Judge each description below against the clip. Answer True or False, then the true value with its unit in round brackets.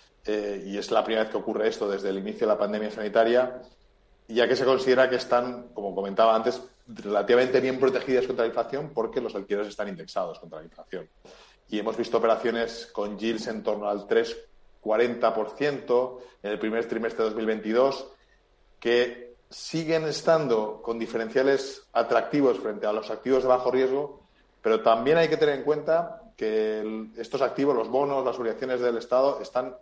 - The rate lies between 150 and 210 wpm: True (175 wpm)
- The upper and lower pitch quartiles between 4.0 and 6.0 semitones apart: False (3.1 semitones)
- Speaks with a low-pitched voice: True (120 Hz)